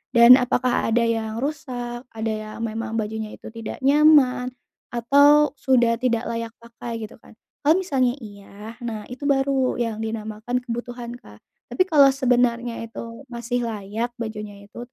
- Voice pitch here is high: Yes, high, 235 Hz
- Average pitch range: No, narrow, 2.2 semitones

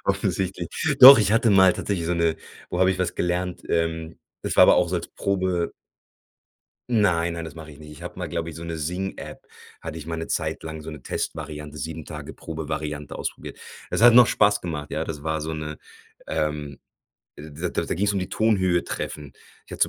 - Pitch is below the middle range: Yes, very low, 85 Hz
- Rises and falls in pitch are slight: No, average, 3.0 semitones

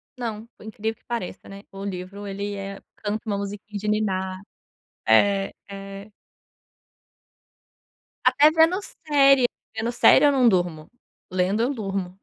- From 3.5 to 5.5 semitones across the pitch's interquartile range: No, average, 2.9 semitones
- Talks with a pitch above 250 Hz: No, high, 205 Hz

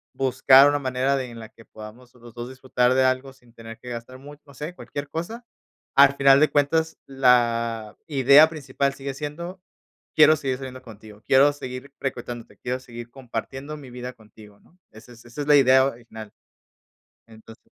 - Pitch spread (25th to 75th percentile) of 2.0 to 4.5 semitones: Yes, average, 2.9 semitones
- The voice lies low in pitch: Yes, low, 130 Hz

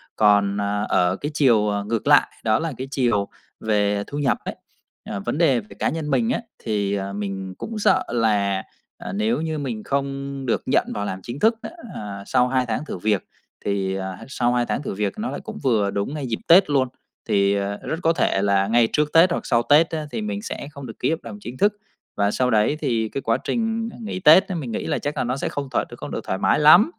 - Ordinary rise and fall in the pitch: No, wide, 6.8 semitones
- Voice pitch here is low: Yes, low, 120 Hz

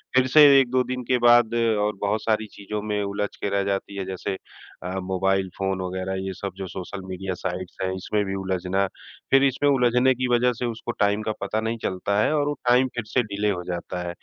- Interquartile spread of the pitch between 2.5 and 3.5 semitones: No, average, 3.9 semitones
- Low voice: Yes, low, 105 Hz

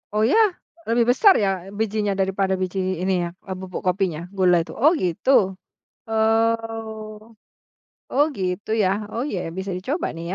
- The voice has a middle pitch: No, high, 210 Hz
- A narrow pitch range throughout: No, average, 3.1 semitones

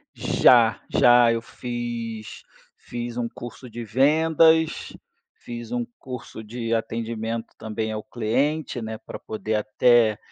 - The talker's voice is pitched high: No, low, 115 Hz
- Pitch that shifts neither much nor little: No, narrow, 1.7 semitones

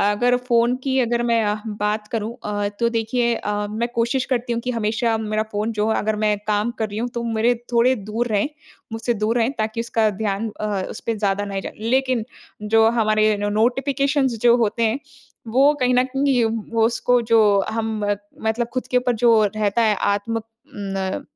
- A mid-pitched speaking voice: No, high, 225 Hz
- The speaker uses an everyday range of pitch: No, narrow, 2.3 semitones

